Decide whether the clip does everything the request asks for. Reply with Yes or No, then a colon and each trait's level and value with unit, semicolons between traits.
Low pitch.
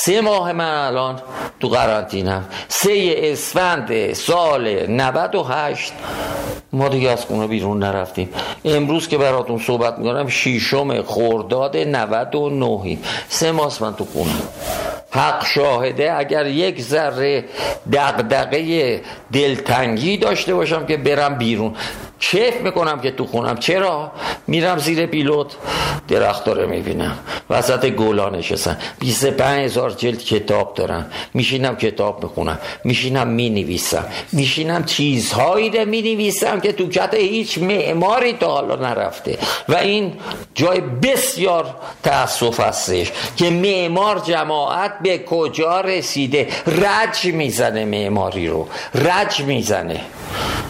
No: medium, 145 Hz